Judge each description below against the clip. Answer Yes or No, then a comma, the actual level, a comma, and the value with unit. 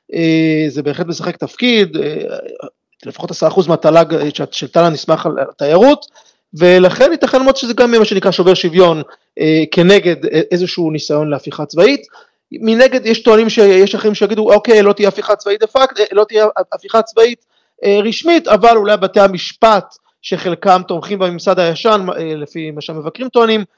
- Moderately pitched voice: No, high, 200 Hz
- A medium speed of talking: No, fast, 160 wpm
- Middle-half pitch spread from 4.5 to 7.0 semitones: Yes, average, 5.2 semitones